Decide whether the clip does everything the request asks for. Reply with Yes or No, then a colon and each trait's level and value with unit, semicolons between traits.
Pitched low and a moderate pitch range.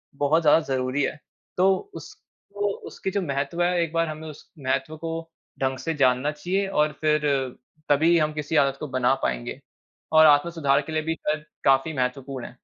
No: medium, 150 Hz; average, 3.0 semitones